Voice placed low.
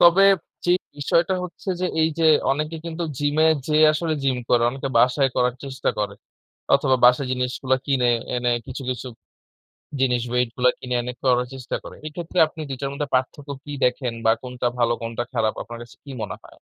Yes: low, 130 Hz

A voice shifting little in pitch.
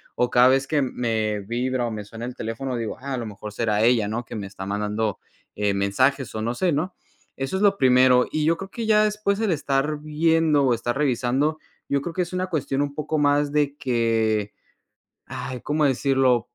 No: average, 4.7 semitones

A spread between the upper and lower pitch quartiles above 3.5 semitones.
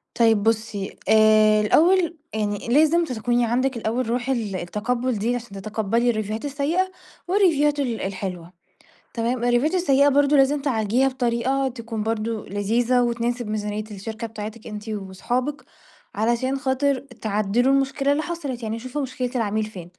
Yes: average, 3.9 semitones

